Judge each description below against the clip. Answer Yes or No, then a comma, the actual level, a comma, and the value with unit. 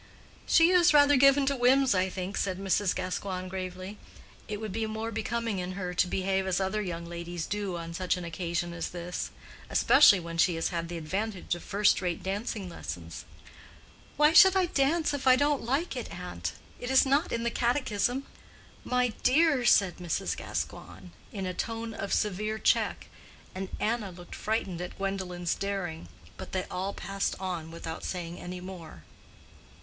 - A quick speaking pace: No, average, 175 wpm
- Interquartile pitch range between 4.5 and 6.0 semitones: Yes, average, 4.8 semitones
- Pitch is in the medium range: No, high, 195 Hz